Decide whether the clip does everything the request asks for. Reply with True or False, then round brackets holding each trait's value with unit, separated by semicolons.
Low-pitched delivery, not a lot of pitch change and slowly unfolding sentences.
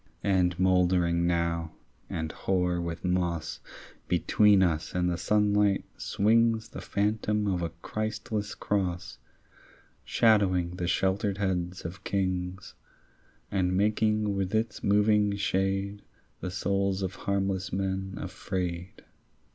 True (95 Hz; 2.3 semitones; 115 wpm)